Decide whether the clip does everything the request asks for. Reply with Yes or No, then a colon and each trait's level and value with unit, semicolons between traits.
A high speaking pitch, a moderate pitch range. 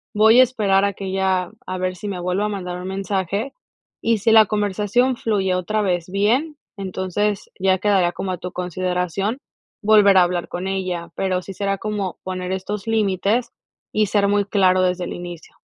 No: high, 195 Hz; narrow, 2.3 semitones